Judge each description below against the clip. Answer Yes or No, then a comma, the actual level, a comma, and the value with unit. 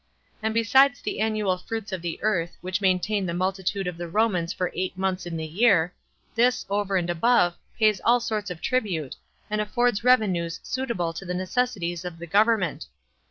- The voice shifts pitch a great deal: No, average, 4.0 semitones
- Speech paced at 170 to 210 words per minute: Yes, average, 180 wpm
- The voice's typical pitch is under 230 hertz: Yes, high, 190 Hz